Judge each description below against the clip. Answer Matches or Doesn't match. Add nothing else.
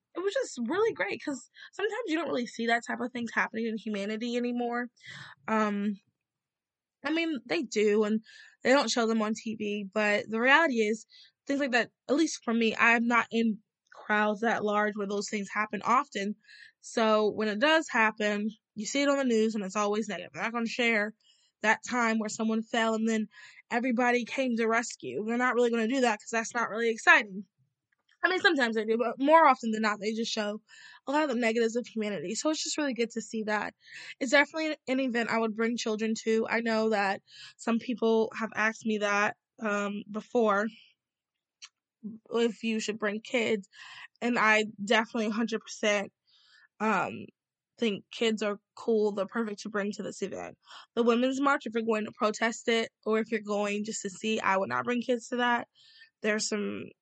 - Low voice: Doesn't match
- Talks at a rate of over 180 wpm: Matches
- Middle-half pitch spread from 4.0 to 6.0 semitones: Doesn't match